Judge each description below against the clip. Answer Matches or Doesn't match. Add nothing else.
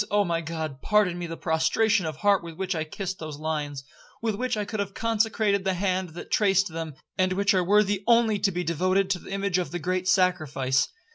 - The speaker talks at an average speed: Doesn't match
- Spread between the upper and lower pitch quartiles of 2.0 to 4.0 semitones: Matches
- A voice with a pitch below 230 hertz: Matches